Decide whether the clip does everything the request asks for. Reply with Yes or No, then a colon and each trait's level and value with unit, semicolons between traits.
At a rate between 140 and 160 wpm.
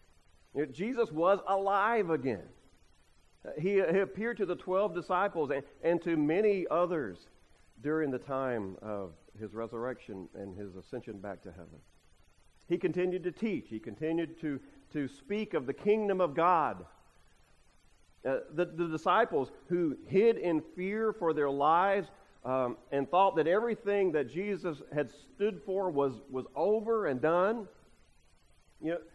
Yes: average, 145 wpm